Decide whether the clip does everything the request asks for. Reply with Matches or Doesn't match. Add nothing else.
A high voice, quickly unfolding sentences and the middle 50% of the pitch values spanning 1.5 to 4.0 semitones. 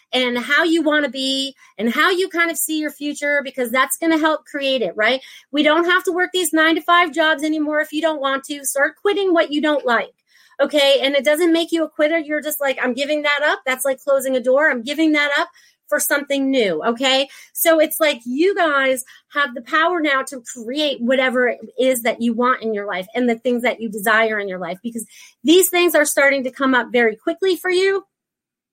Matches